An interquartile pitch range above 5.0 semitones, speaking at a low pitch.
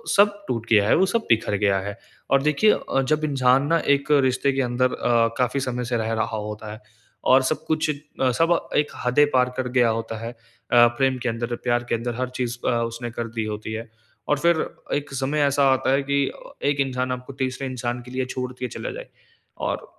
No: average, 2.8 semitones; low, 125 Hz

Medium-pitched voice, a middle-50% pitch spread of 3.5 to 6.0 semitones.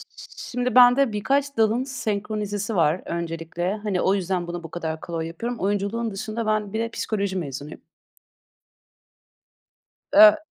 No: high, 205 Hz; average, 4.9 semitones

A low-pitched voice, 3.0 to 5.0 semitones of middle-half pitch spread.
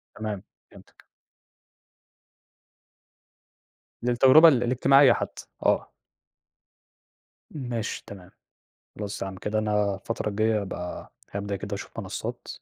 Yes: low, 105 Hz; average, 3.3 semitones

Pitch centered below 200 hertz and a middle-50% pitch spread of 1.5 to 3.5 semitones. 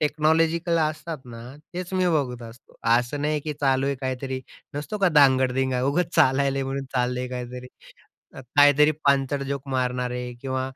Yes: low, 135 Hz; average, 2.9 semitones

